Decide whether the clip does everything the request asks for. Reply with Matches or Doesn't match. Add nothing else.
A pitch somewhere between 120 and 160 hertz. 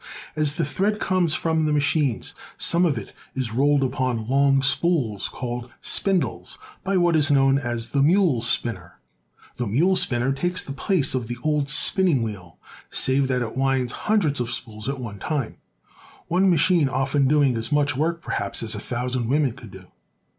Matches